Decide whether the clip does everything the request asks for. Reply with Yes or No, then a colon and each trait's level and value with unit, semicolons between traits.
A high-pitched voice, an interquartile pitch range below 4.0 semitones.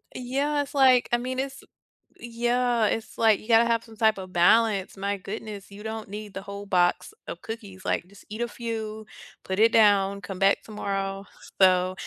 Yes: high, 215 Hz; average, 3.0 semitones